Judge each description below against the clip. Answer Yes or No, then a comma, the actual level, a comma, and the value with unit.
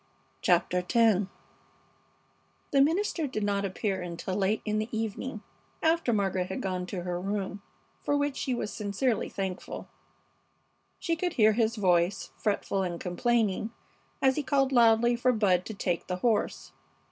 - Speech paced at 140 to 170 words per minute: Yes, average, 150 wpm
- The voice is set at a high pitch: Yes, high, 210 Hz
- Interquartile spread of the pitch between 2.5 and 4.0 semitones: No, average, 4.6 semitones